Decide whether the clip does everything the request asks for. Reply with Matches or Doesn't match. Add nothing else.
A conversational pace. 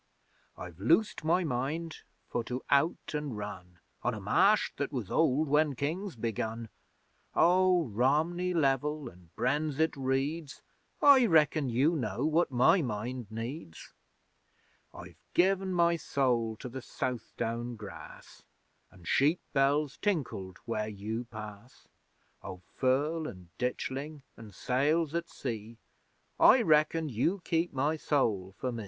Doesn't match